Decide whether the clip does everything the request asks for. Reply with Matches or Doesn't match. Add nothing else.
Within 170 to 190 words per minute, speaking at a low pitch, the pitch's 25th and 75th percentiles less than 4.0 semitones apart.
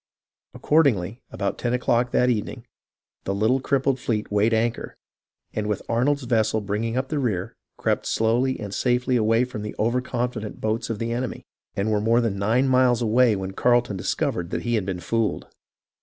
Matches